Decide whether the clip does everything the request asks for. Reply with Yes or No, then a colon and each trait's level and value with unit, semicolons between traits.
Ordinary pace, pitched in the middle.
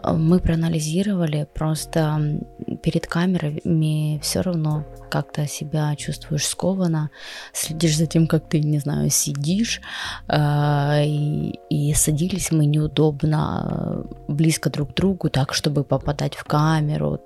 Yes: average, 115 wpm; medium, 155 Hz